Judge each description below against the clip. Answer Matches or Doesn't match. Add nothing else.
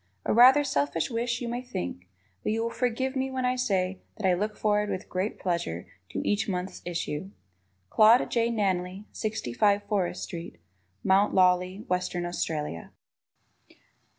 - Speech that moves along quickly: Doesn't match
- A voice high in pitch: Matches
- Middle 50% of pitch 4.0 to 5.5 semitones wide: Matches